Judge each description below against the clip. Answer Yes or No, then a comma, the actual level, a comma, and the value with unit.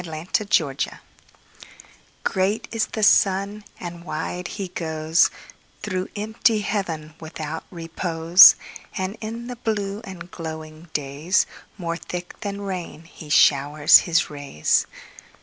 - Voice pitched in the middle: Yes, medium, 175 Hz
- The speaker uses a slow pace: Yes, slow, 105 wpm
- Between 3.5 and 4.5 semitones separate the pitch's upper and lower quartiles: Yes, average, 4.0 semitones